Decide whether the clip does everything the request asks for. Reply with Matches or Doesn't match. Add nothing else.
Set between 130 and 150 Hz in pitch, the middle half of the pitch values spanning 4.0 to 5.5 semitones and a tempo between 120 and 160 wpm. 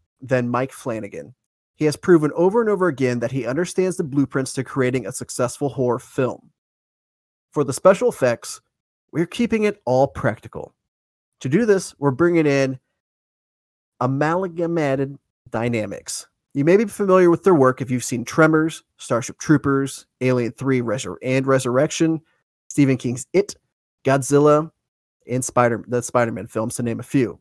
Matches